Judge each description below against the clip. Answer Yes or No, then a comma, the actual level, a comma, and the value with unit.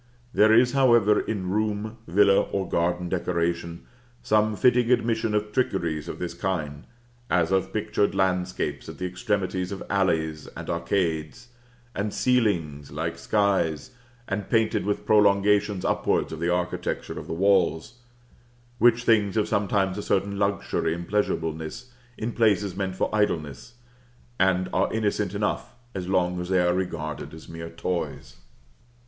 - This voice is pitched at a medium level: No, very low, 95 Hz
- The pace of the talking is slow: No, average, 145 wpm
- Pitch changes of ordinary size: Yes, average, 3.5 semitones